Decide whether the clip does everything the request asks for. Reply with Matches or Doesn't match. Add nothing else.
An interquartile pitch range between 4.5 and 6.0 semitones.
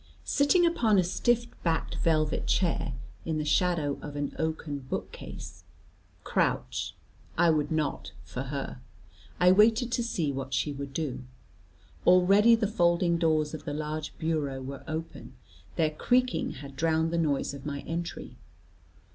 Doesn't match